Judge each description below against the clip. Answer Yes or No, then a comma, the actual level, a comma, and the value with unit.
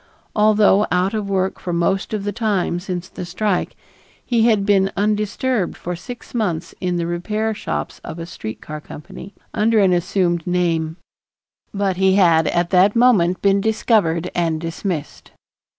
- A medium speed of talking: Yes, average, 160 wpm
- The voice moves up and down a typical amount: Yes, average, 3.4 semitones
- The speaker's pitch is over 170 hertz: Yes, high, 190 Hz